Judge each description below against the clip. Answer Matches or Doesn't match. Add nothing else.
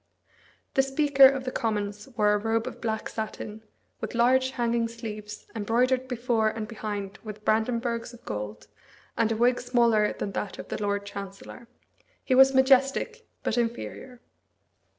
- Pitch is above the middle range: Matches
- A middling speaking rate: Matches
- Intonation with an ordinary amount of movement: Matches